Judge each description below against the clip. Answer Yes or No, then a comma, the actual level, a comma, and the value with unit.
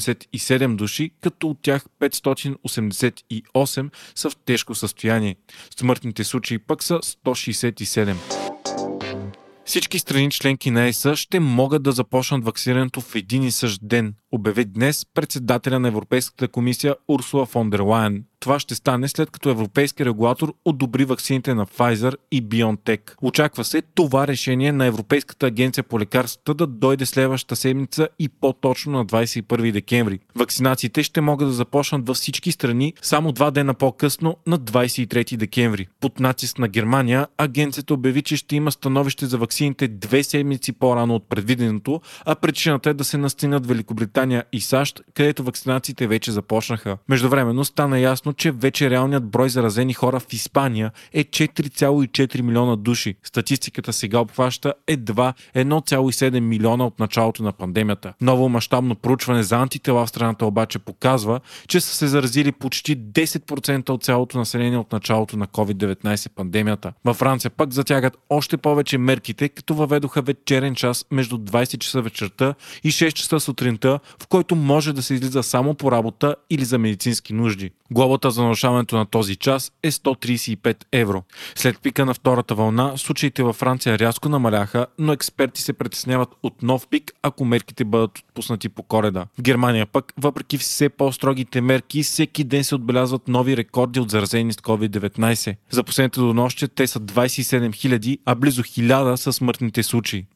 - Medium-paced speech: Yes, average, 155 wpm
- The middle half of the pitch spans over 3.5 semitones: No, average, 3.2 semitones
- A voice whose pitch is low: Yes, low, 130 Hz